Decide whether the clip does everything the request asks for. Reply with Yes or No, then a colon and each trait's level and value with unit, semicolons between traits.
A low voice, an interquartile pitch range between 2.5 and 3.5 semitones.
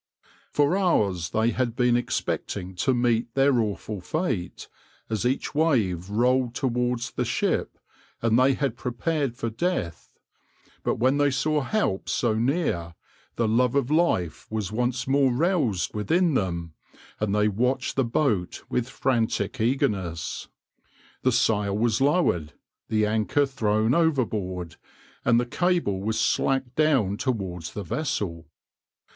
No: low, 120 Hz; average, 4.6 semitones